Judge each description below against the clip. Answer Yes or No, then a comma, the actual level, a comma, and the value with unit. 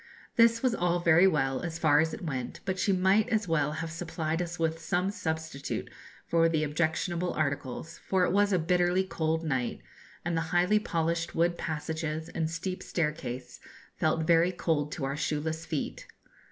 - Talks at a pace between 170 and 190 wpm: Yes, average, 175 wpm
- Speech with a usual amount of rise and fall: No, narrow, 2.2 semitones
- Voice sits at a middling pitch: Yes, medium, 165 Hz